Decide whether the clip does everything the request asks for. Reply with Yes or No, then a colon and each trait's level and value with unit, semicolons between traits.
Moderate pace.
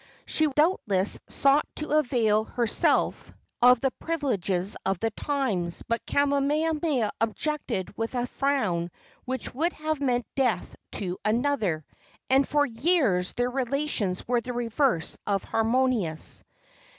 No: slow, 125 wpm